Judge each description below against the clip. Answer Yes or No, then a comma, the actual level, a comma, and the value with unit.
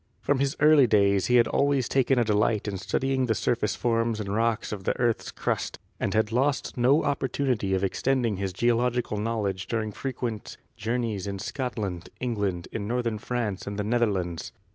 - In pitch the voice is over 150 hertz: No, low, 115 Hz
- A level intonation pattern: No, average, 3.5 semitones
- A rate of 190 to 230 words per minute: No, average, 175 wpm